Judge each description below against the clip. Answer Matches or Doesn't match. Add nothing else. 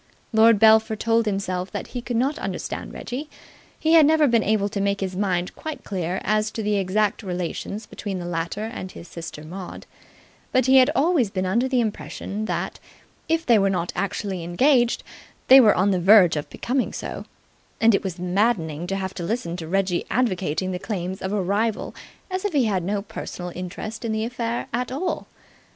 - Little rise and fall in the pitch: Doesn't match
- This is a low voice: Doesn't match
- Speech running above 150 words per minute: Matches